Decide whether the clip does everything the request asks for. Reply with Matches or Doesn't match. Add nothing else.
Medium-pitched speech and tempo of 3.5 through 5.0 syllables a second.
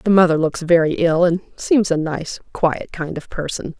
Matches